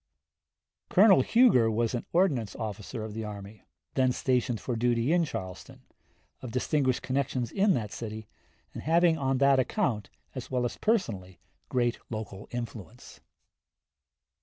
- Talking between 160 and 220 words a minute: No, slow, 135 wpm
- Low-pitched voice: Yes, low, 120 Hz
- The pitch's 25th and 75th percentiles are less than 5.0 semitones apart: Yes, average, 4.0 semitones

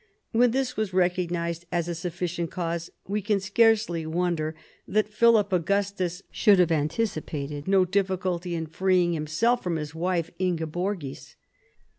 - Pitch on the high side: No, medium, 180 Hz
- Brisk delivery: No, average, 145 wpm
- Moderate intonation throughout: Yes, average, 3.2 semitones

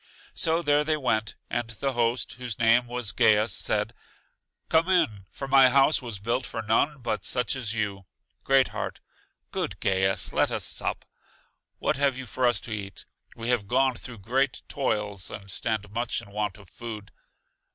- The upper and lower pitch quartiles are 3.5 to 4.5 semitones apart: Yes, average, 4.1 semitones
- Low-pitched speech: Yes, low, 120 Hz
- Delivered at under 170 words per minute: No, average, 175 wpm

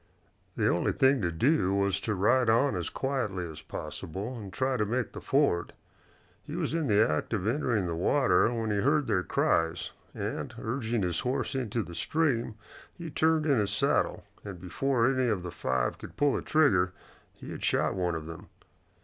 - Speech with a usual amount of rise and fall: No, wide, 6.5 semitones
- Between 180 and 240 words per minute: Yes, average, 190 wpm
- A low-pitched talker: Yes, low, 110 Hz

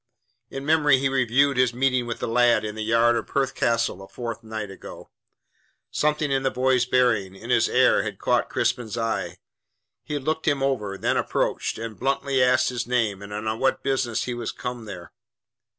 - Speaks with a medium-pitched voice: No, low, 125 Hz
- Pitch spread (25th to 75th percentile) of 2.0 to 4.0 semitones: Yes, average, 3.2 semitones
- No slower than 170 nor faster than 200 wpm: Yes, average, 190 wpm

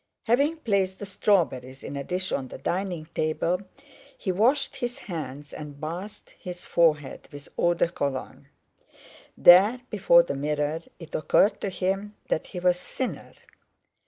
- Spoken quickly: No, average, 150 wpm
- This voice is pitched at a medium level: Yes, medium, 175 Hz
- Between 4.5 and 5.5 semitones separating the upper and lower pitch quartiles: Yes, average, 4.8 semitones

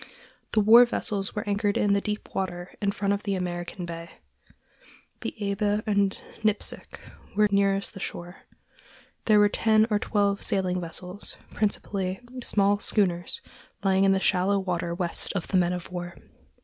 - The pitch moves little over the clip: Yes, narrow, 2.3 semitones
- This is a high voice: Yes, high, 195 Hz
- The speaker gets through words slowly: No, average, 160 wpm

